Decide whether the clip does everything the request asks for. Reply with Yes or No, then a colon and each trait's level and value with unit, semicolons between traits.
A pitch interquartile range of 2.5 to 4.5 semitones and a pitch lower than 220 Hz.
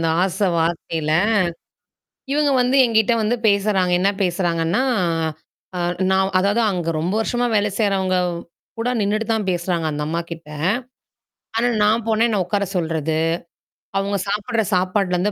Yes: average, 3.8 semitones; high, 195 Hz